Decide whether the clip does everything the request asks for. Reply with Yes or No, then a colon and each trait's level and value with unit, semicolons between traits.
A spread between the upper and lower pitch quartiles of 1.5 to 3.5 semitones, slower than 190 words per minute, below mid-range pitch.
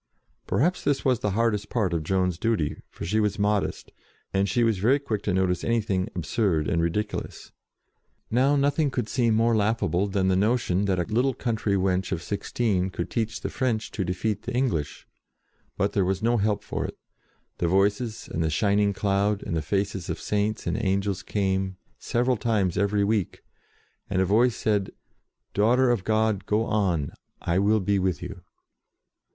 Yes: average, 3.1 semitones; average, 180 wpm; low, 100 Hz